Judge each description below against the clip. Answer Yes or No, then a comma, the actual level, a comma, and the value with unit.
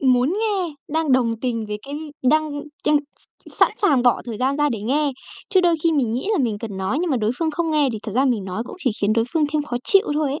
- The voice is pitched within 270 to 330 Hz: Yes, very high, 275 Hz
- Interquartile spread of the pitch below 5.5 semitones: Yes, average, 5.1 semitones